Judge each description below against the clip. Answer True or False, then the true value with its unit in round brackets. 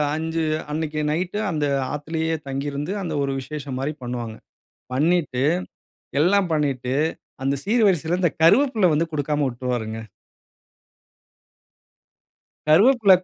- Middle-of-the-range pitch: True (155 Hz)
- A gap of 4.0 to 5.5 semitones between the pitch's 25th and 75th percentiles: True (4.4 semitones)